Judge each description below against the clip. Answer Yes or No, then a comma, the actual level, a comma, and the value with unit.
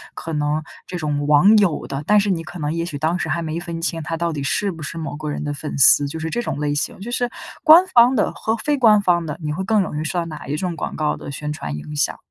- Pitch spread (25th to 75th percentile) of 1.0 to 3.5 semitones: No, average, 4.1 semitones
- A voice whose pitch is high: No, medium, 165 Hz